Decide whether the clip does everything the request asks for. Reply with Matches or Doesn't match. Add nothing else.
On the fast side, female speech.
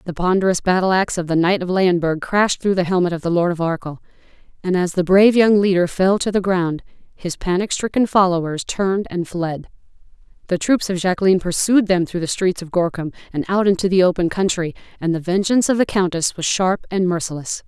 Matches